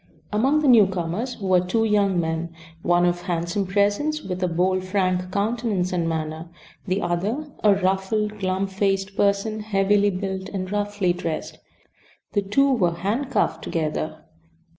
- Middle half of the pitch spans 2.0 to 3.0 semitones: Yes, average, 2.7 semitones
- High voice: Yes, high, 195 Hz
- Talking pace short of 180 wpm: Yes, average, 140 wpm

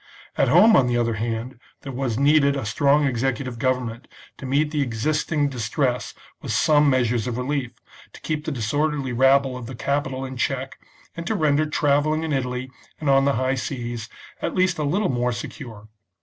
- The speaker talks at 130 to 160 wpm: No, average, 185 wpm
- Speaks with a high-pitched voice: No, low, 135 Hz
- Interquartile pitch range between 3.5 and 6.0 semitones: No, average, 3.1 semitones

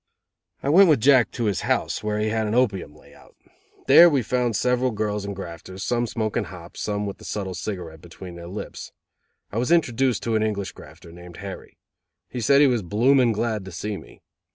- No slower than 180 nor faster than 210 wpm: Yes, average, 200 wpm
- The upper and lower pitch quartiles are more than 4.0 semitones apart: Yes, average, 4.4 semitones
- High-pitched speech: No, low, 105 Hz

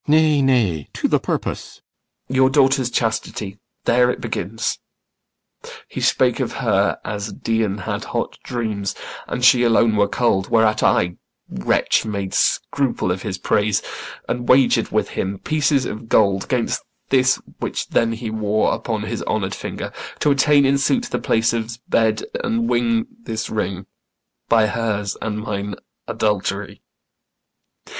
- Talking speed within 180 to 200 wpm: No, average, 150 wpm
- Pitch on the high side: No, low, 115 Hz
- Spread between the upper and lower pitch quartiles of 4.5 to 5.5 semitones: No, average, 4.1 semitones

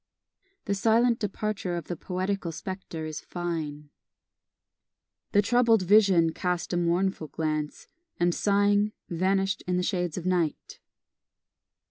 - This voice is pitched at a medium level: Yes, medium, 180 Hz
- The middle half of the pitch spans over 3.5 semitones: No, average, 3.0 semitones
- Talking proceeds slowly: Yes, slow, 120 wpm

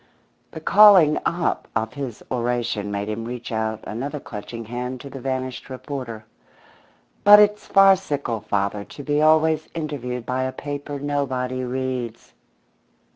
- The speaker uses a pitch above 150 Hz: No, low, 130 Hz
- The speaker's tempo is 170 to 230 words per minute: No, slow, 135 wpm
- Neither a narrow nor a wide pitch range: Yes, average, 4.1 semitones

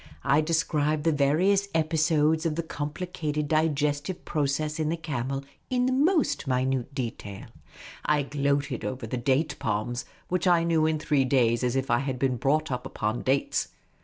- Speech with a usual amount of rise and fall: Yes, average, 3.2 semitones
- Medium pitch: Yes, medium, 150 Hz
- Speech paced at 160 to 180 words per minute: Yes, average, 165 wpm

